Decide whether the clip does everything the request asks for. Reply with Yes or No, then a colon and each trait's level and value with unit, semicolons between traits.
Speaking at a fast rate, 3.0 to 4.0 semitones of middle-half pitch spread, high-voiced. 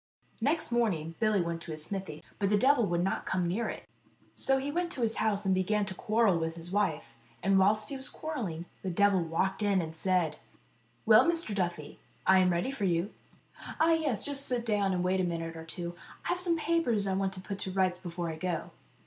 No: fast, 225 wpm; average, 4.8 semitones; high, 195 Hz